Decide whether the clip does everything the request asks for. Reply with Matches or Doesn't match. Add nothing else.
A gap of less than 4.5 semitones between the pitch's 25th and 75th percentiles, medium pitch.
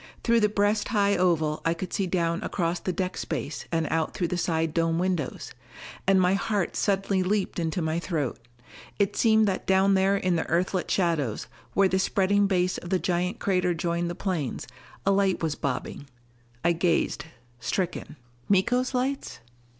Matches